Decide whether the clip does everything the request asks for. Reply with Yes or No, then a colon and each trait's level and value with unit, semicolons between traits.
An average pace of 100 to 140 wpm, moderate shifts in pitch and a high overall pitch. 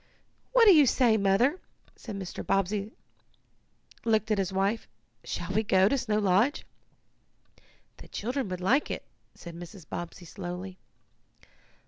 Yes: slow, 135 wpm; average, 3.7 semitones; high, 200 Hz